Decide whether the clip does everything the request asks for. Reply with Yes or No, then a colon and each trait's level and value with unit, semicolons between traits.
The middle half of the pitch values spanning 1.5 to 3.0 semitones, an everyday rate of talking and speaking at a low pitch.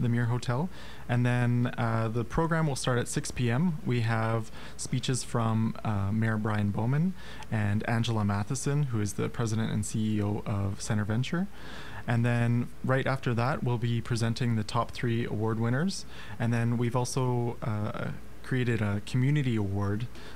Yes: narrow, 2.5 semitones; average, 160 wpm; low, 120 Hz